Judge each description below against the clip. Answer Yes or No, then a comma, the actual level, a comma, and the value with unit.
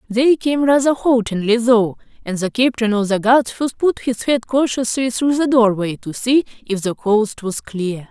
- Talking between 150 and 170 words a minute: No, average, 190 wpm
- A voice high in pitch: Yes, high, 235 Hz